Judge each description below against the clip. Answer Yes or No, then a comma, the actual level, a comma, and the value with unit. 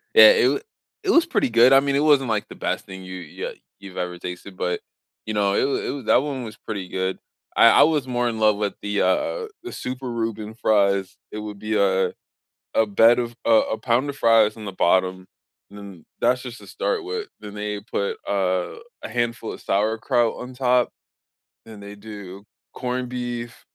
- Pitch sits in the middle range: No, low, 110 Hz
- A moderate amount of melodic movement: Yes, average, 3.9 semitones